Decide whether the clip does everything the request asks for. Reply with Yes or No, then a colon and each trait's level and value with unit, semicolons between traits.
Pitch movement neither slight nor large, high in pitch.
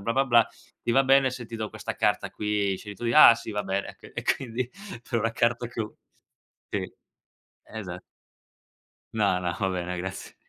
No: average, 3.3 semitones; low, 115 Hz